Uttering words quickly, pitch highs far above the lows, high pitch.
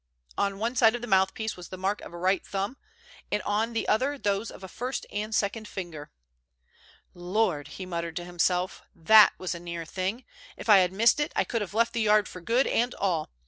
No: fast, 220 wpm; average, 3.7 semitones; high, 200 Hz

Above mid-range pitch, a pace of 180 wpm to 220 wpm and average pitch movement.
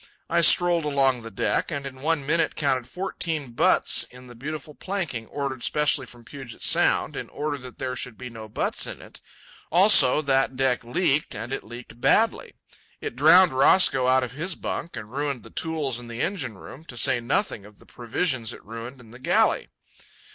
No: low, 135 Hz; average, 190 wpm; average, 4.0 semitones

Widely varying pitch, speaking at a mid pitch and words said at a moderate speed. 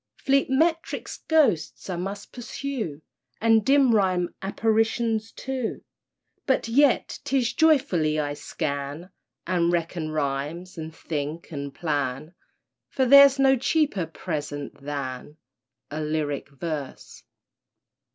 No: wide, 8.8 semitones; medium, 180 Hz; slow, 110 wpm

